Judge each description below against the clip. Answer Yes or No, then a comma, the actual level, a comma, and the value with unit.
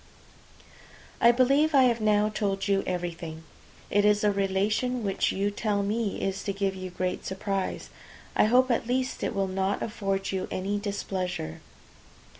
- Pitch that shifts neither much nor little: No, narrow, 2.2 semitones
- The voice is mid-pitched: No, high, 200 Hz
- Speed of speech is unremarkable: Yes, average, 160 wpm